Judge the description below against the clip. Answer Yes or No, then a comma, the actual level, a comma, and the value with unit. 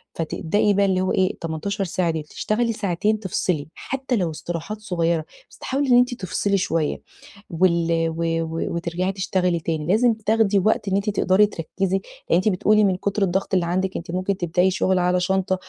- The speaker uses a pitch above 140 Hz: Yes, medium, 185 Hz